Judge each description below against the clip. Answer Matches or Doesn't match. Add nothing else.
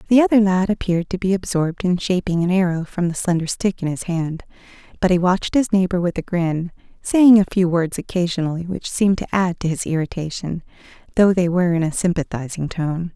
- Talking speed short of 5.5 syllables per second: Doesn't match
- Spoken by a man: Doesn't match